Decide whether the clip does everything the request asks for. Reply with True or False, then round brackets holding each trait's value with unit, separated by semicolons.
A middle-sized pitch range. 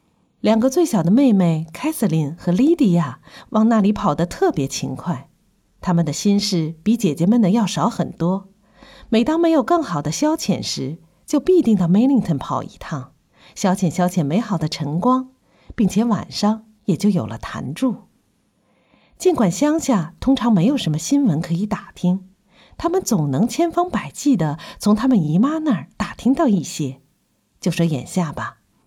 False (6.8 semitones)